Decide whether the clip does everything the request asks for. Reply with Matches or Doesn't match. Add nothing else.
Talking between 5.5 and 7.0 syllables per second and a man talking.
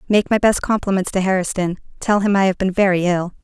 Doesn't match